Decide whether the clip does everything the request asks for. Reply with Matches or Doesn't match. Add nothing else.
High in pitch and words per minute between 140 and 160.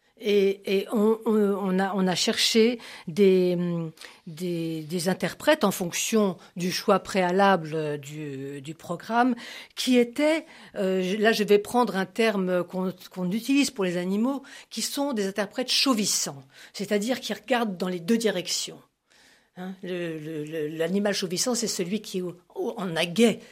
Matches